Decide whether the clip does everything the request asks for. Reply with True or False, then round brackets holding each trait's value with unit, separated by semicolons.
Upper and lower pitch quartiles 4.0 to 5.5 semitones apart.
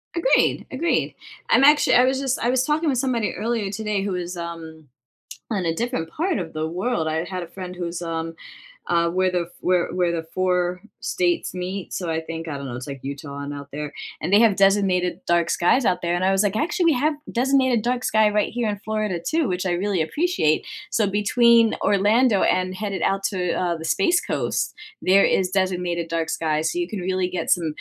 True (5.0 semitones)